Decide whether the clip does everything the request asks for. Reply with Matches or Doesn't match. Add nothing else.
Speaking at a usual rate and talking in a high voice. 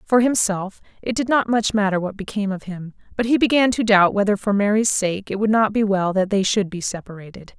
Doesn't match